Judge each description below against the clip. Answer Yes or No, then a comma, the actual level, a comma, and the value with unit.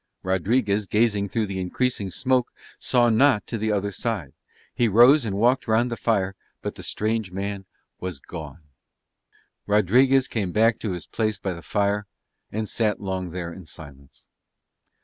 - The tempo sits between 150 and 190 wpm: Yes, average, 160 wpm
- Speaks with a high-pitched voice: No, low, 105 Hz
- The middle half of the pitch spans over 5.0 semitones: No, average, 3.6 semitones